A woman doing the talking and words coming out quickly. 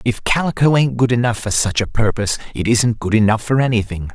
No: male; fast, 215 wpm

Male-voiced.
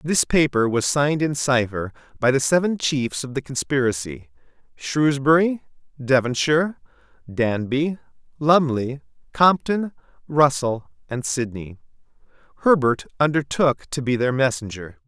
Yes: male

